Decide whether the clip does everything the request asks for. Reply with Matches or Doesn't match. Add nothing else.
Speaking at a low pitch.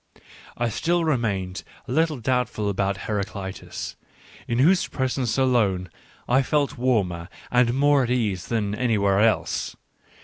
Matches